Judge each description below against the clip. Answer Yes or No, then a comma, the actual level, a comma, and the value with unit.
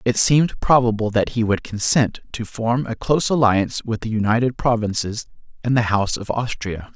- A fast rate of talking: No, average, 180 wpm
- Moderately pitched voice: No, low, 115 Hz